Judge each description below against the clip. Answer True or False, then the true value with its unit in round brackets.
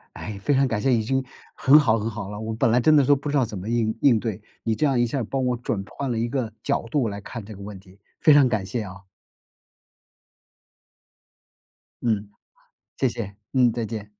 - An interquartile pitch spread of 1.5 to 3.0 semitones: False (3.8 semitones)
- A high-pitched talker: False (115 Hz)